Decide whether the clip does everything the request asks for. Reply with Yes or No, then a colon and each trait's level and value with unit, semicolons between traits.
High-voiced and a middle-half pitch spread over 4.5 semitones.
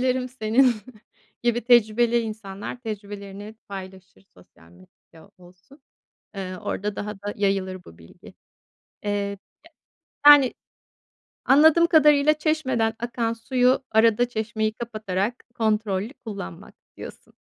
No: high, 220 Hz; average, 3.8 semitones